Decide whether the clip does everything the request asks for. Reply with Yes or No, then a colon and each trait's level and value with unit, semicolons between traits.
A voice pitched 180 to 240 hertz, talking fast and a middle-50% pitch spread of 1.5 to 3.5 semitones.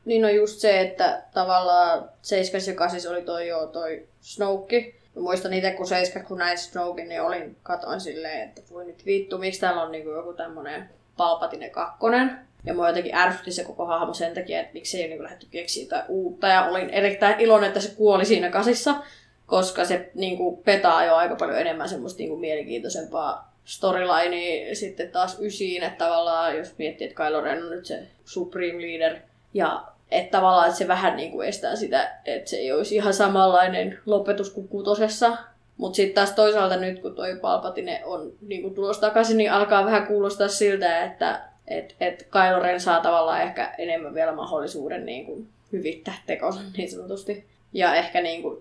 Yes: medium, 185 Hz; fast, 180 wpm; average, 3.0 semitones